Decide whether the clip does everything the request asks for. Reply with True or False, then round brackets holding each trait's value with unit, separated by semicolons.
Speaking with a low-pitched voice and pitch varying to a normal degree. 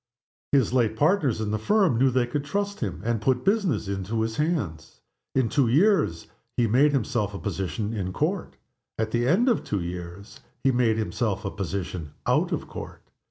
False (115 Hz; 5.8 semitones)